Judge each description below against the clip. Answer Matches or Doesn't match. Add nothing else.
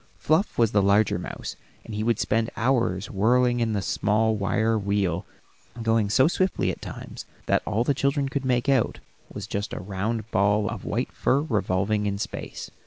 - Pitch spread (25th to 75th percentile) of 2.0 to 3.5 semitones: Matches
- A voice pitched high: Doesn't match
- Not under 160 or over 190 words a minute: Matches